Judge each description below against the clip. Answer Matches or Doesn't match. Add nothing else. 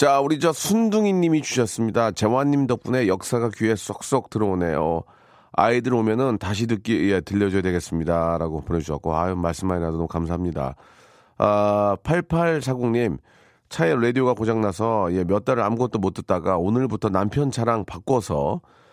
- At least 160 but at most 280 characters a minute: Doesn't match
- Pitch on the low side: Matches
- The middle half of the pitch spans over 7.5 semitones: Doesn't match